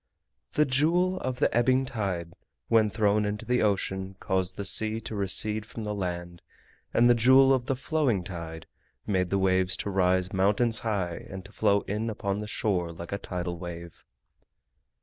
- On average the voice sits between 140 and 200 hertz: No, low, 100 Hz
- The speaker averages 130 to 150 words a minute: No, average, 175 wpm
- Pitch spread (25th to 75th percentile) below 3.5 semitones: No, average, 3.8 semitones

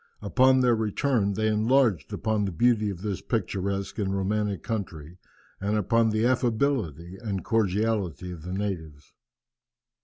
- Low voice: Yes, low, 105 Hz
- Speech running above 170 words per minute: No, average, 140 wpm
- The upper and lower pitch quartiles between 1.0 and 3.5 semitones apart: Yes, average, 3.2 semitones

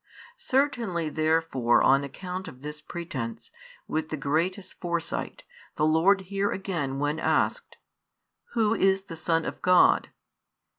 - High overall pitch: No, medium, 165 Hz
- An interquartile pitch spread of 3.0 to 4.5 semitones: Yes, average, 4.1 semitones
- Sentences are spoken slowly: Yes, slow, 130 wpm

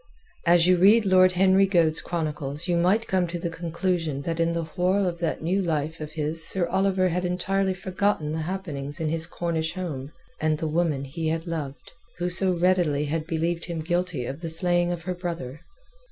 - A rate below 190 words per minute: No, average, 195 wpm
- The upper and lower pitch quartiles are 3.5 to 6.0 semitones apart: No, narrow, 2.5 semitones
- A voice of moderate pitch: Yes, medium, 170 Hz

